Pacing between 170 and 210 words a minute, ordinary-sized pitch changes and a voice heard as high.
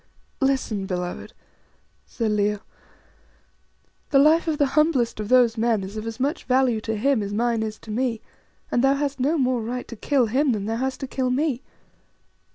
Yes: average, 185 wpm; average, 3.7 semitones; high, 245 Hz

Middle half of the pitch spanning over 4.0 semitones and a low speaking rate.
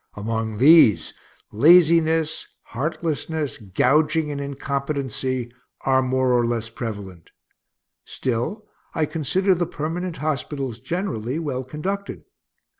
Yes: average, 5.1 semitones; slow, 100 wpm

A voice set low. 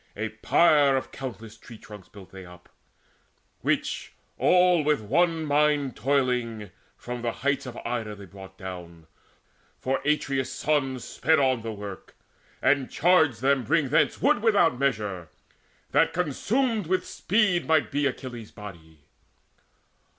Yes: low, 130 Hz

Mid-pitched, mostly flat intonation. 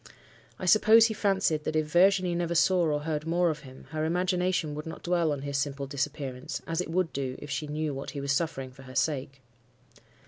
No: medium, 155 Hz; average, 3.9 semitones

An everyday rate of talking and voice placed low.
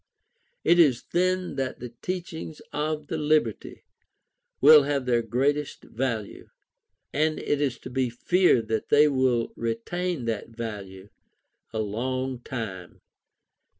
No: slow, 125 wpm; low, 130 Hz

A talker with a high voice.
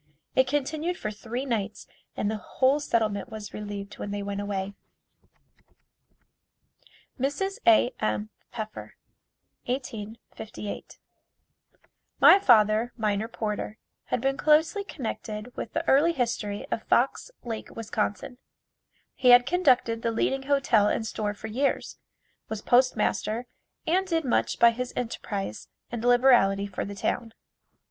Yes: high, 230 Hz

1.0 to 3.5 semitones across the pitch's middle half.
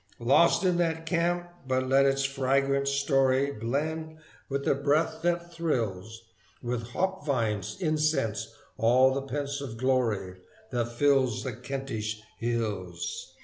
No: average, 4.6 semitones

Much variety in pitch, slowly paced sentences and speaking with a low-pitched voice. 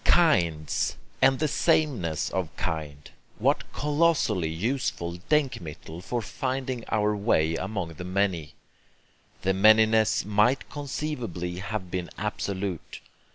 Yes: wide, 6.8 semitones; slow, 105 wpm; low, 100 Hz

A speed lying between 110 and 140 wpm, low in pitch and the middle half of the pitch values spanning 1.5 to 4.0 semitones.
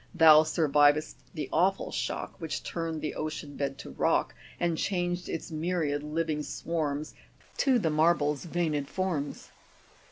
No: slow, 135 wpm; medium, 155 Hz; narrow, 2.5 semitones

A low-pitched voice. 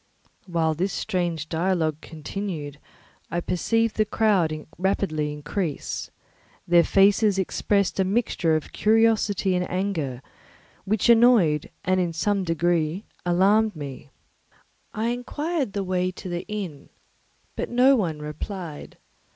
No: medium, 185 Hz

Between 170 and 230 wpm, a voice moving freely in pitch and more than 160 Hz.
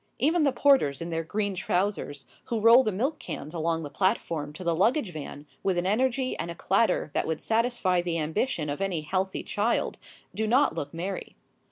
Yes: average, 195 wpm; wide, 5.9 semitones; medium, 185 Hz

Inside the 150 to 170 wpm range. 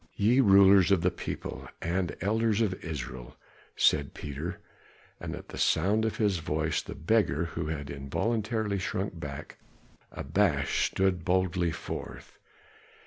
No: slow, 135 wpm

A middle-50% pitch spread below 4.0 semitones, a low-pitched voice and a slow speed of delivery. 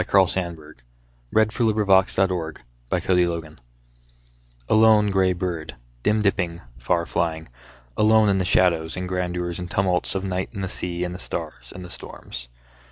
No: narrow, 2.4 semitones; very low, 90 Hz; average, 155 wpm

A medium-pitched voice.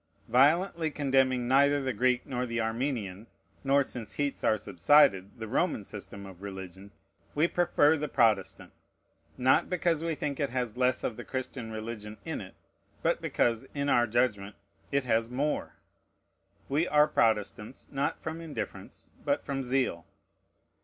No: low, 125 Hz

